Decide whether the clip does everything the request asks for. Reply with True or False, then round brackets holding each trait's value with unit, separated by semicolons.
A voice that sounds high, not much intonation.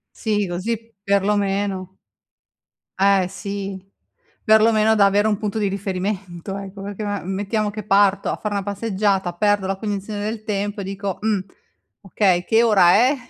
True (200 Hz; 1.5 semitones)